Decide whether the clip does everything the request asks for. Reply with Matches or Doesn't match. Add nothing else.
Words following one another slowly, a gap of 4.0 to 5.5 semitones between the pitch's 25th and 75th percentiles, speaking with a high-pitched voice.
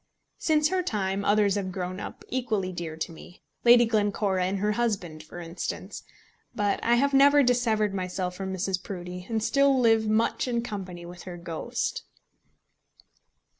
Doesn't match